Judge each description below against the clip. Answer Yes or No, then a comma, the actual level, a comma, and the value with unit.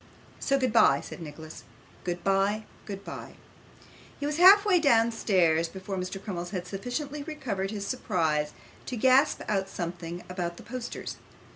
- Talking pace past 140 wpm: No, slow, 135 wpm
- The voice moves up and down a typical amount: No, wide, 6.4 semitones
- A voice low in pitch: No, high, 195 Hz